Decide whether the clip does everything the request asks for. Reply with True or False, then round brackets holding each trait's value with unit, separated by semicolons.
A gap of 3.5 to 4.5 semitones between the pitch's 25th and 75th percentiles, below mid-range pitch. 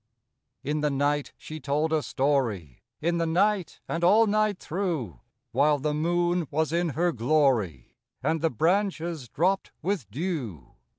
False (3.9 semitones; 155 Hz)